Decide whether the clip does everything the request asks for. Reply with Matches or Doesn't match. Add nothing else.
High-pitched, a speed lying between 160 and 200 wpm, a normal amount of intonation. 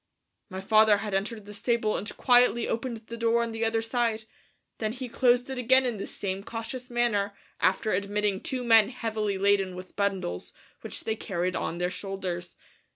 Matches